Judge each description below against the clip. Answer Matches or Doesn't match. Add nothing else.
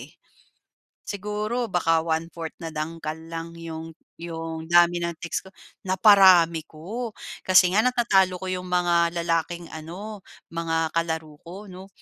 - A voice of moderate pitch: Matches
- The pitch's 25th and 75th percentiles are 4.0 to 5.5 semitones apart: Doesn't match